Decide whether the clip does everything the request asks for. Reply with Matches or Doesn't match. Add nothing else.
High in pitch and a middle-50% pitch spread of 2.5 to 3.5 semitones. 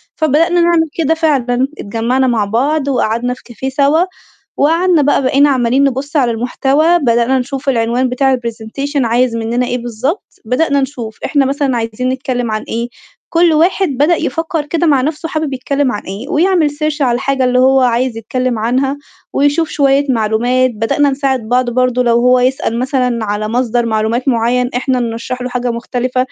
Matches